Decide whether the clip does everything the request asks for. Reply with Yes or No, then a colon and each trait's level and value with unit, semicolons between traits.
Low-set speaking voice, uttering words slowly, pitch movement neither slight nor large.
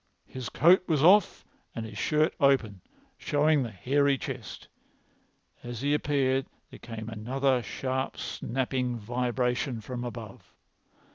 Yes: low, 130 Hz; slow, 125 wpm; average, 3.0 semitones